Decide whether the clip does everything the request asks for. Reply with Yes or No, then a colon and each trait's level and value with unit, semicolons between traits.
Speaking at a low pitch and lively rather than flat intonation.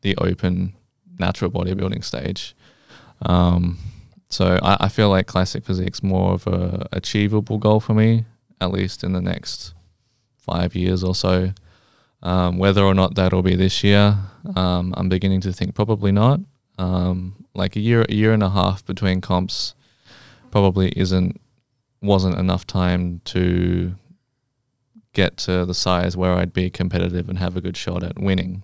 No: very low, 95 Hz; average, 2.8 semitones